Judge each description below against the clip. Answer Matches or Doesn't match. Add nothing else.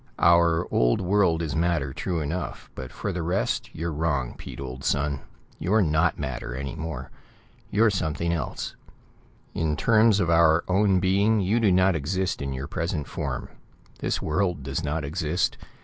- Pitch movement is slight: Doesn't match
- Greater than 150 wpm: Matches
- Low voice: Matches